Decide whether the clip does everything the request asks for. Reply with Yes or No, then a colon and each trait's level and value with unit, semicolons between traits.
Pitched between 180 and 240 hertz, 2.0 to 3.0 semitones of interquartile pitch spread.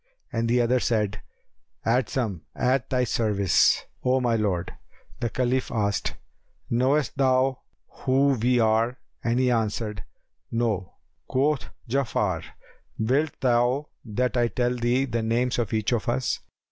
No: low, 120 Hz; narrow, 2.6 semitones